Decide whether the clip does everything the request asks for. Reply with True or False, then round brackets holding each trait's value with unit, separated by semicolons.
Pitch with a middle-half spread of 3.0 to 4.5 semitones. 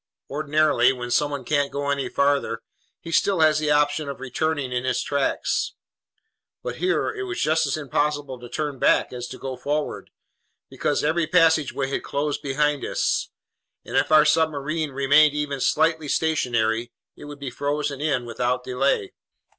False (2.5 semitones)